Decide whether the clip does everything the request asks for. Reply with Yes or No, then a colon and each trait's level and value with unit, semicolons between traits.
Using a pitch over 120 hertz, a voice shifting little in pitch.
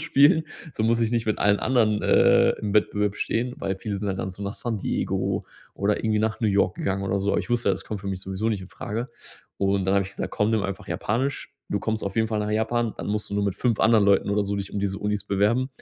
No: low, 105 Hz; narrow, 2.0 semitones